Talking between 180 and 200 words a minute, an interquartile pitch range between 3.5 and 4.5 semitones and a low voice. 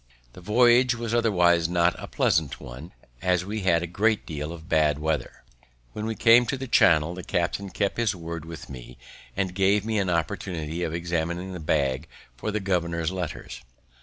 Yes: average, 185 wpm; average, 4.1 semitones; very low, 90 Hz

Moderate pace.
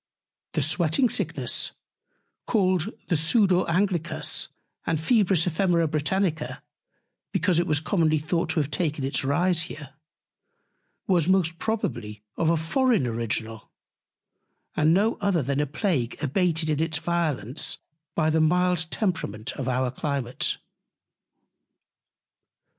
No: slow, 120 wpm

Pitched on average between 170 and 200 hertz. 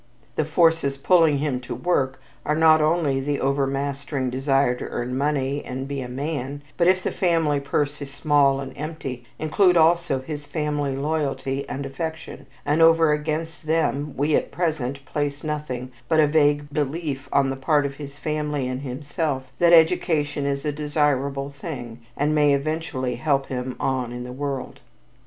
No: medium, 145 Hz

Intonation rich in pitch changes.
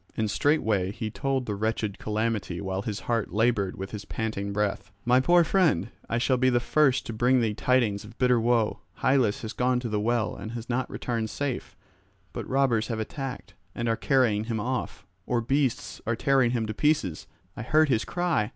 No: average, 3.2 semitones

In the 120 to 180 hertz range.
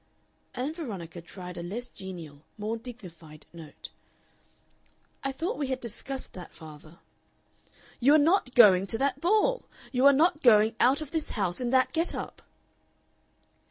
No: high, 240 Hz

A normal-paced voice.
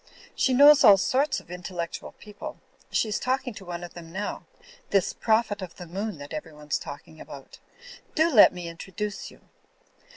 Yes: average, 170 wpm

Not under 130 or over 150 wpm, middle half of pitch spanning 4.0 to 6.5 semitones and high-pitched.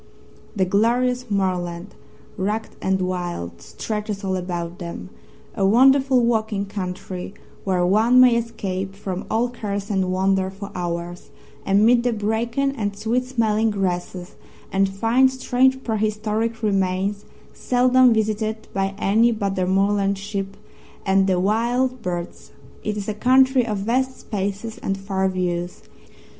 No: slow, 135 wpm; average, 3.4 semitones; high, 205 Hz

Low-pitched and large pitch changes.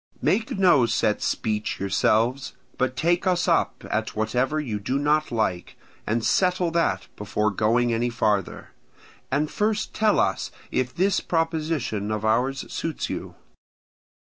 Yes: low, 130 Hz; wide, 7.1 semitones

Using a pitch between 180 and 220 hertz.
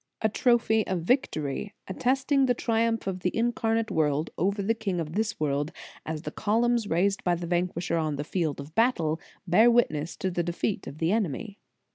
Yes: high, 190 Hz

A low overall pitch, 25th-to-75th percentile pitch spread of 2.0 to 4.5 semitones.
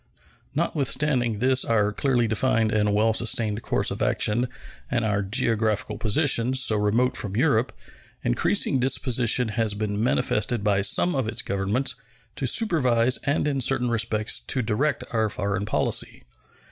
Yes: low, 115 Hz; average, 3.4 semitones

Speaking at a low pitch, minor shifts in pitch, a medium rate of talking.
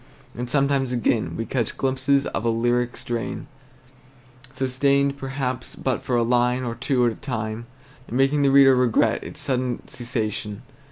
Yes: low, 125 Hz; narrow, 2.3 semitones; average, 160 wpm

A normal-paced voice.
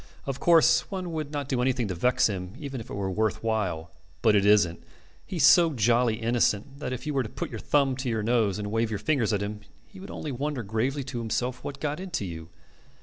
No: fast, 235 wpm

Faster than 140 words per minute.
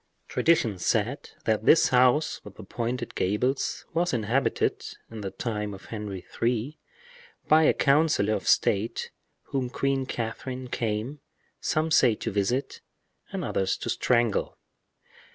No: slow, 135 wpm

